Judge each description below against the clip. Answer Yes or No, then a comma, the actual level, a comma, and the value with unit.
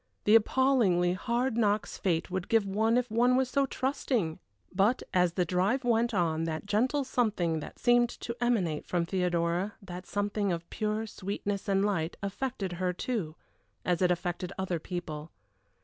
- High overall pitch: Yes, high, 200 Hz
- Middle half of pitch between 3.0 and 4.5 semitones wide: No, average, 4.9 semitones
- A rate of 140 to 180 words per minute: Yes, average, 165 wpm